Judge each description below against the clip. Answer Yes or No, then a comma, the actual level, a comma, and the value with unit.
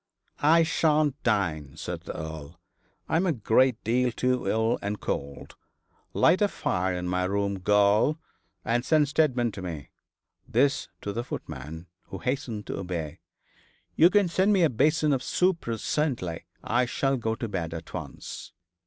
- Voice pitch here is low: Yes, low, 115 Hz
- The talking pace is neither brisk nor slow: Yes, average, 165 wpm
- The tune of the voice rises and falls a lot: Yes, wide, 8.0 semitones